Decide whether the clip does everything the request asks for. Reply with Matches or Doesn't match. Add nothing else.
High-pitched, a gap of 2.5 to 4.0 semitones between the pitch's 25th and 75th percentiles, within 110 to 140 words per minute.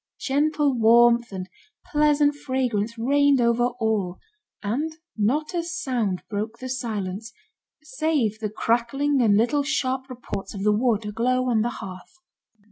Doesn't match